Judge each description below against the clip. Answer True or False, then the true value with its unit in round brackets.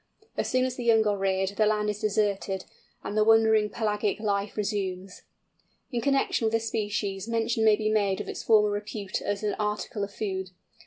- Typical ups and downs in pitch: False (1.7 semitones)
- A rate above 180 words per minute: True (195 wpm)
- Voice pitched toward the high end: True (210 Hz)